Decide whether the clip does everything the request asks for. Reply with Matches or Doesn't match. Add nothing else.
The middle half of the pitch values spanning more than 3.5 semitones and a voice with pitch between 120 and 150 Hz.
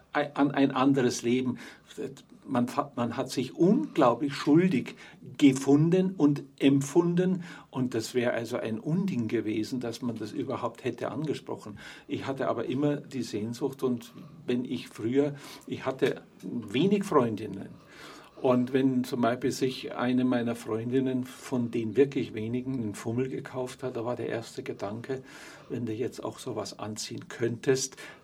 Doesn't match